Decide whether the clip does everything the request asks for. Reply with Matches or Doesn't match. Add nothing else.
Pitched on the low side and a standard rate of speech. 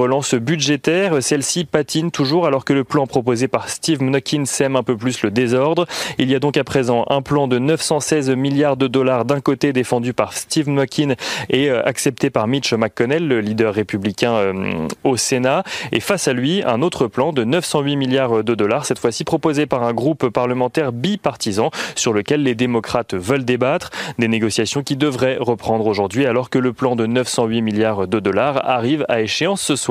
Matches